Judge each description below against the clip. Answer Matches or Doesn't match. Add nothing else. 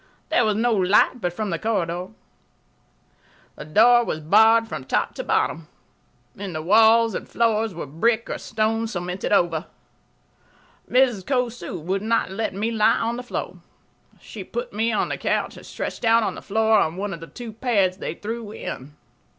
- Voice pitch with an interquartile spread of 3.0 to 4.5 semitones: Matches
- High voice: Matches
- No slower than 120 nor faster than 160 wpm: Doesn't match